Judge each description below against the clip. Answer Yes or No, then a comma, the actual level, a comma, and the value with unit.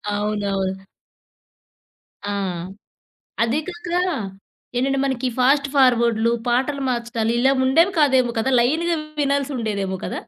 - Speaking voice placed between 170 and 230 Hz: No, very high, 250 Hz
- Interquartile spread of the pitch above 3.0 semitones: Yes, average, 3.7 semitones